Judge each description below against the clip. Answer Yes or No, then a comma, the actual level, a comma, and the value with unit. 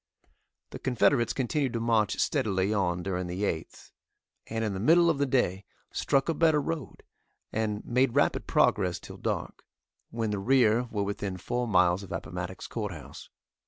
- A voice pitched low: Yes, low, 110 Hz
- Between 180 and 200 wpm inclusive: No, average, 160 wpm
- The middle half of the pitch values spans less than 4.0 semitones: No, average, 4.9 semitones